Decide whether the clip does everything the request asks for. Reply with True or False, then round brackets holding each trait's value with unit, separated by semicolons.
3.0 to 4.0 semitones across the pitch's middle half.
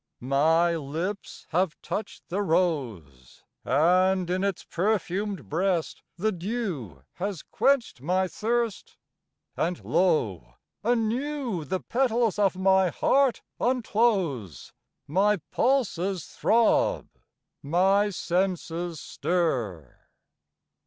False (4.7 semitones)